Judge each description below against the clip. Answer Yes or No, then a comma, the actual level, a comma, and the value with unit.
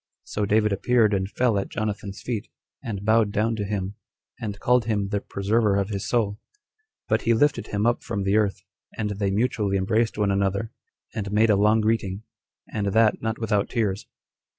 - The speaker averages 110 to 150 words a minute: No, average, 185 wpm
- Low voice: Yes, low, 105 Hz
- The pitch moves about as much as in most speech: No, narrow, 2.0 semitones